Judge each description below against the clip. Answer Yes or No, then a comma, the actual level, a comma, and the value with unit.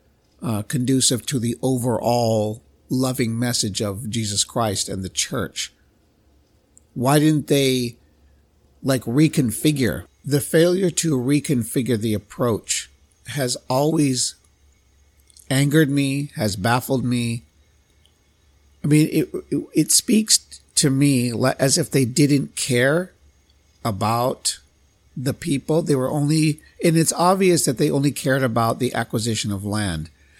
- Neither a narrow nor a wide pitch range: No, wide, 6.2 semitones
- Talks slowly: Yes, slow, 120 wpm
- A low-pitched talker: Yes, low, 125 Hz